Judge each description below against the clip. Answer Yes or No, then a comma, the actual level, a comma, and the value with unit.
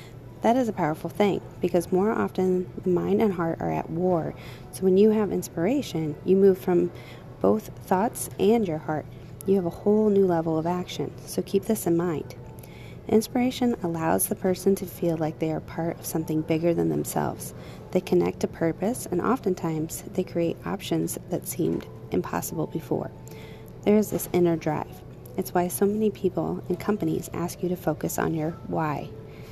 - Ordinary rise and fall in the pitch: Yes, average, 3.5 semitones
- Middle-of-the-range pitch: Yes, medium, 175 Hz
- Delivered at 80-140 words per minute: No, average, 180 wpm